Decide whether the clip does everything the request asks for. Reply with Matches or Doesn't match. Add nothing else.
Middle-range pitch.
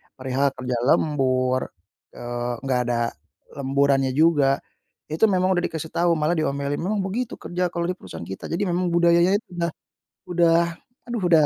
Matches